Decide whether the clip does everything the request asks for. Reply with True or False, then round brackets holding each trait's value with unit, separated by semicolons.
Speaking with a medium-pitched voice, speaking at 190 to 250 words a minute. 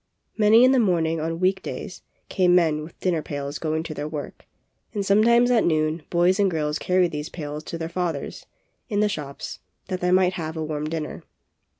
True (170 Hz; 200 wpm)